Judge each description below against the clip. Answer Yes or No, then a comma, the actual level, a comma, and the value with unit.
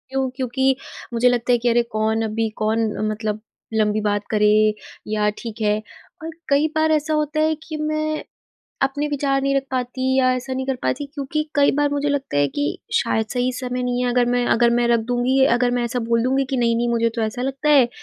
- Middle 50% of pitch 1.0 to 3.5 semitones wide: Yes, average, 3.2 semitones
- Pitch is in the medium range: No, very high, 250 Hz